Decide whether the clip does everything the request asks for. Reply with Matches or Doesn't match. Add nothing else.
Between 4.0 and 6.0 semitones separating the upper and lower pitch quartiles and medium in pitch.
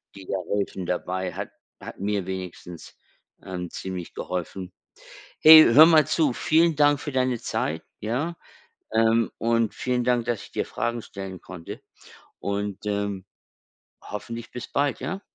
Doesn't match